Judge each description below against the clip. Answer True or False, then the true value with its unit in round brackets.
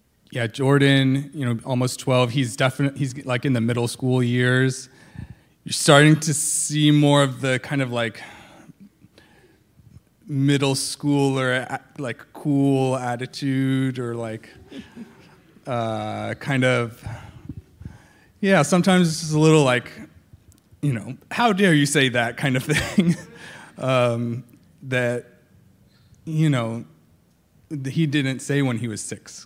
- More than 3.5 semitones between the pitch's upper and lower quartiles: False (3.1 semitones)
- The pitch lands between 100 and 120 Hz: False (135 Hz)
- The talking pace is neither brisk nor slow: False (130 wpm)